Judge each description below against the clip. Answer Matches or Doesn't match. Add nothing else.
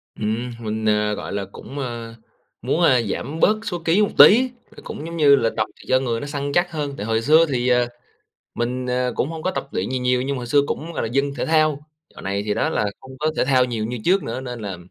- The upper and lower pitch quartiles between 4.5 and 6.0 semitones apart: Matches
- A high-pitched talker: Doesn't match